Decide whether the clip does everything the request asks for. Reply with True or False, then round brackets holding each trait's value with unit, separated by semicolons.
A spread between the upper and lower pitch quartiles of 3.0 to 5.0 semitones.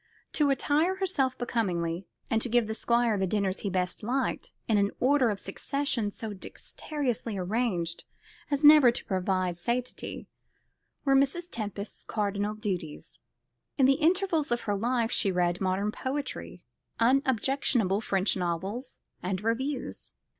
False (5.6 semitones)